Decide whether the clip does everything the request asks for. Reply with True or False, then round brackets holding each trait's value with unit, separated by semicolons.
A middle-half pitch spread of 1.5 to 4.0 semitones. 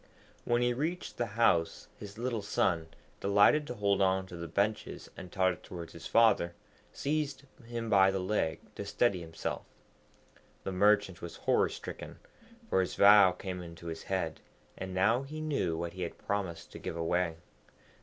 False (4.6 semitones)